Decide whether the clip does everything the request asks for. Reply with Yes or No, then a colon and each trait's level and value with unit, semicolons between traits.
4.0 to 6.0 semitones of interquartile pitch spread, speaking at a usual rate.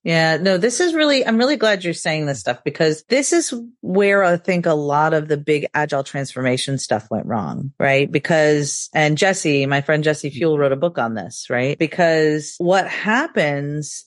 Yes: average, 4.9 semitones; average, 190 wpm